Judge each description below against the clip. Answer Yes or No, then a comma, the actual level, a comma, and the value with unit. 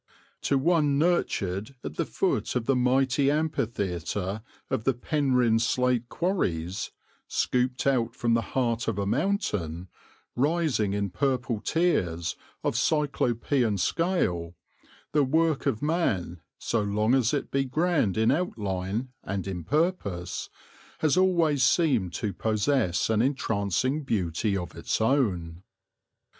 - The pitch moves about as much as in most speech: No, wide, 6.3 semitones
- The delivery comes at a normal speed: No, slow, 125 wpm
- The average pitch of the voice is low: Yes, low, 120 Hz